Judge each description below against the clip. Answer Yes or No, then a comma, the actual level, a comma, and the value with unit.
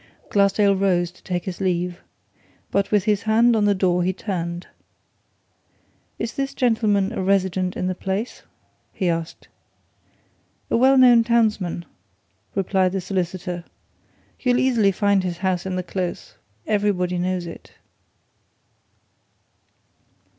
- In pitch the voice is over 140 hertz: Yes, high, 190 Hz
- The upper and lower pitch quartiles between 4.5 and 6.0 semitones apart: No, average, 2.8 semitones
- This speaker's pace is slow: Yes, slow, 125 wpm